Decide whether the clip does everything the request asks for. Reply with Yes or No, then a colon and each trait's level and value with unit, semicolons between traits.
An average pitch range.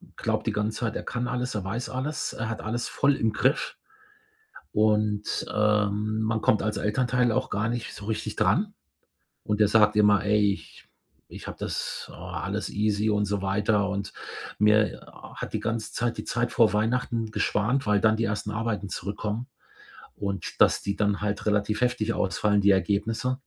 No: narrow, 1.9 semitones